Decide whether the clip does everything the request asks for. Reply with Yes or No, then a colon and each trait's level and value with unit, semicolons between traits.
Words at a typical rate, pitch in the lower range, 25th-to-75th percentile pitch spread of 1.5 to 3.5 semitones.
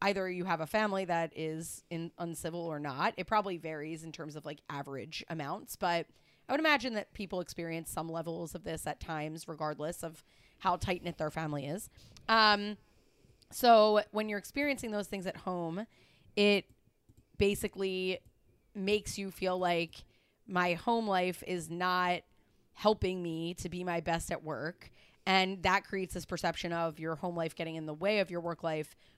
No: average, 175 wpm; medium, 175 Hz; average, 3.2 semitones